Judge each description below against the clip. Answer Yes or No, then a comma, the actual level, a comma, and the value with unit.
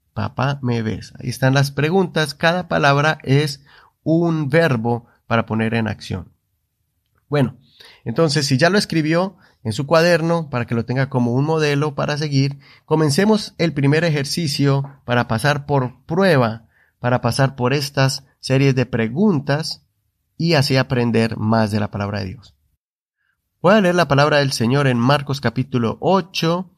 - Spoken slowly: No, average, 155 wpm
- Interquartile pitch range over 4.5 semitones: Yes, average, 5.0 semitones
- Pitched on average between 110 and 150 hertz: Yes, low, 135 Hz